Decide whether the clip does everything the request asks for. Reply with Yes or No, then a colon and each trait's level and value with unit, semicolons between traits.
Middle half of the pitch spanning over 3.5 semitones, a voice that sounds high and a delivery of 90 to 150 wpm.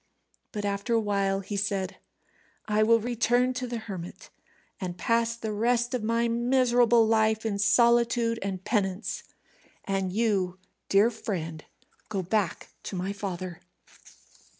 No: average, 3.2 semitones; high, 215 Hz; slow, 135 wpm